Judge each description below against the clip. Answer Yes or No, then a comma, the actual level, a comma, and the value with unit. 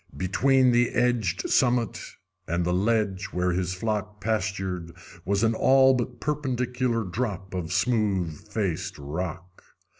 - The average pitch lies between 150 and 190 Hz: No, low, 105 Hz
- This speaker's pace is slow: Yes, slow, 125 wpm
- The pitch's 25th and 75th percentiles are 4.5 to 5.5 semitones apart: Yes, average, 5.0 semitones